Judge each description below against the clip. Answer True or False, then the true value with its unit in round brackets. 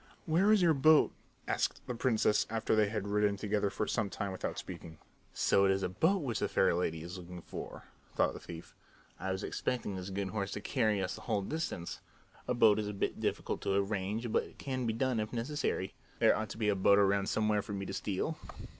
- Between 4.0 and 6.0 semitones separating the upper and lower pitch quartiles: False (3.2 semitones)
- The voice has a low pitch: True (105 Hz)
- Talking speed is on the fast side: True (225 wpm)